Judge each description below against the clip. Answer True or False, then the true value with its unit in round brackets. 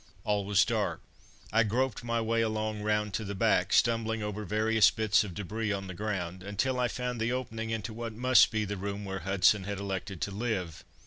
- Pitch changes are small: True (2.1 semitones)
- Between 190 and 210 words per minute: True (205 wpm)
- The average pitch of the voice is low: True (105 Hz)